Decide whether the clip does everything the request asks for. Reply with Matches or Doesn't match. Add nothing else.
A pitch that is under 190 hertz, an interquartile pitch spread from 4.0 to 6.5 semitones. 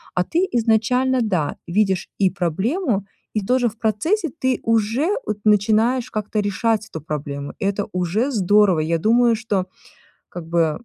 Doesn't match